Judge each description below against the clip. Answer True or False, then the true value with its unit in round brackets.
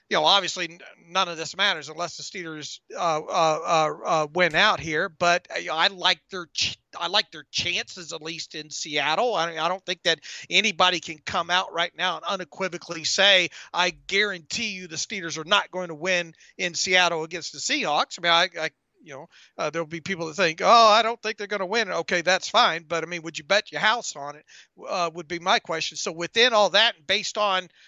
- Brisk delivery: True (225 wpm)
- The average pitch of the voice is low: False (175 Hz)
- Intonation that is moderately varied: True (3.1 semitones)